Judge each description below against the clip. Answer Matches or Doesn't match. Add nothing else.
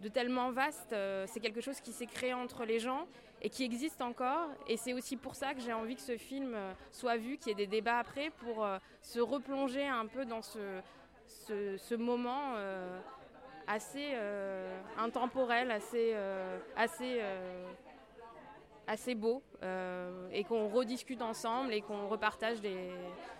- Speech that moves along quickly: Doesn't match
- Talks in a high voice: Matches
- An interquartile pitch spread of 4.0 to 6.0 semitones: Doesn't match